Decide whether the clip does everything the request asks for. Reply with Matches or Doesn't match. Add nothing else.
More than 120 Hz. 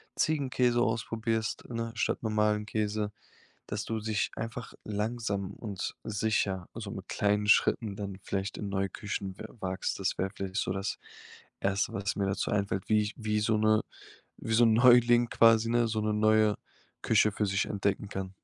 Doesn't match